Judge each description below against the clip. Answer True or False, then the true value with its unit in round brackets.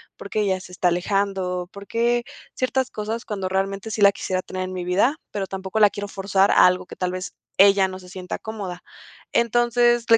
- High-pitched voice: True (195 Hz)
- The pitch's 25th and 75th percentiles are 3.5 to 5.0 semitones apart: False (2.9 semitones)